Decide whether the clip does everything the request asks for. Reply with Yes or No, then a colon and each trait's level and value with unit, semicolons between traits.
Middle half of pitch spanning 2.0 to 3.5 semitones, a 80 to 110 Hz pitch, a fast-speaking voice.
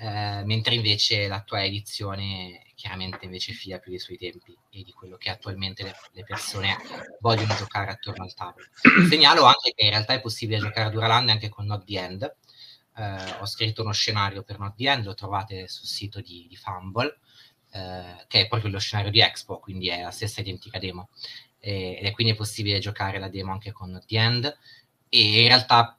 Yes: average, 2.8 semitones; low, 105 Hz; fast, 200 wpm